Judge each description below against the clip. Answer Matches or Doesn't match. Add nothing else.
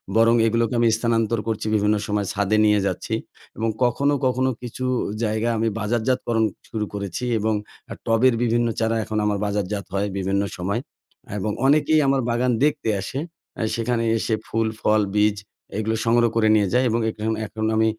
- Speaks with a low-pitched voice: Matches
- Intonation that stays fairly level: Matches